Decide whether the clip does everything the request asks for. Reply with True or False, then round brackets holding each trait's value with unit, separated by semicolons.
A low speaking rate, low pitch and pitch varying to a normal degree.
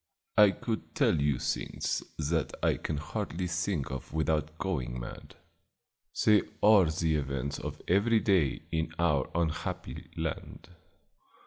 True (130 wpm; 80 Hz; 4.6 semitones)